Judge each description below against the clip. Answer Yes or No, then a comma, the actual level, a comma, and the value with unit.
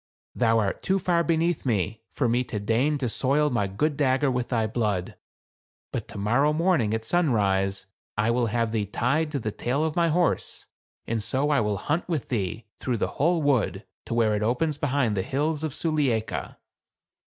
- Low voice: Yes, low, 125 Hz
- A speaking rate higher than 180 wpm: Yes, average, 190 wpm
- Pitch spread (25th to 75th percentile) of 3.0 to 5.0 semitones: No, wide, 5.6 semitones